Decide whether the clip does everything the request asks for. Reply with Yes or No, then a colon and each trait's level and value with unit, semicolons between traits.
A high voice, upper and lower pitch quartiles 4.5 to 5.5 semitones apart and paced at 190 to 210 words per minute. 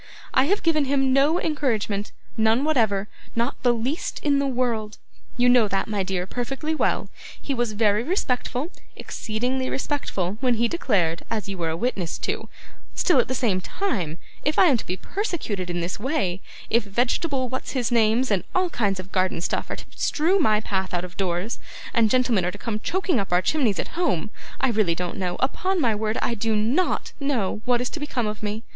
Yes: high, 230 Hz; average, 5.2 semitones; average, 200 wpm